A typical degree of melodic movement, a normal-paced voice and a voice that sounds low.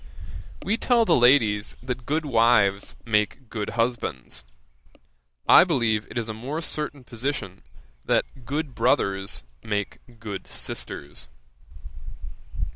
No: average, 4.9 semitones; slow, 115 wpm; low, 115 Hz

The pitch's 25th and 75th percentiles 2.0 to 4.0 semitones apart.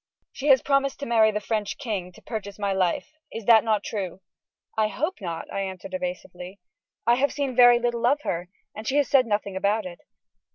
No: average, 4.4 semitones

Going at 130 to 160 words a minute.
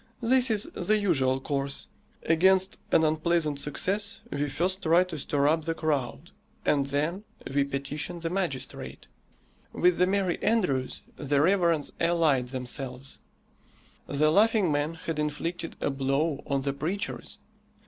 Yes: average, 140 wpm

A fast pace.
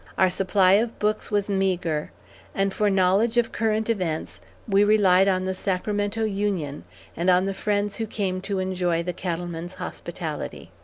No: average, 160 wpm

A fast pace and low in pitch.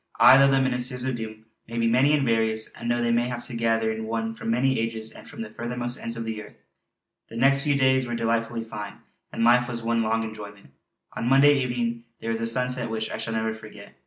Yes: fast, 245 wpm; low, 115 Hz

